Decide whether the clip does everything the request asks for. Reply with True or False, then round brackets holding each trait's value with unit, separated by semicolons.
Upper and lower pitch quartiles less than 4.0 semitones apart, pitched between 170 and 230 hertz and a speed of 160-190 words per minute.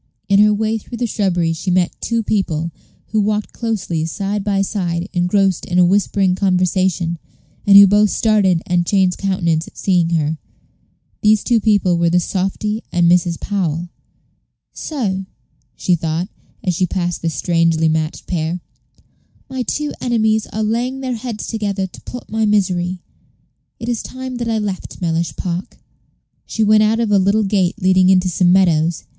True (3.5 semitones; 190 Hz; 165 wpm)